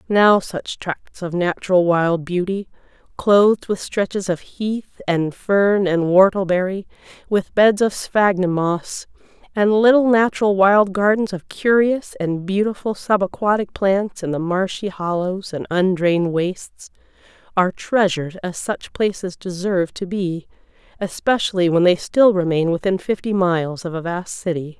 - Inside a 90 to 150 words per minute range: Yes, average, 145 wpm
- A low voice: No, high, 190 Hz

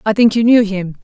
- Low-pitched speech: No, high, 210 Hz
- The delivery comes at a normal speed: No, fast, 290 wpm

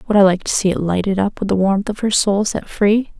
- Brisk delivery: Yes, fast, 300 wpm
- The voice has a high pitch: Yes, high, 200 Hz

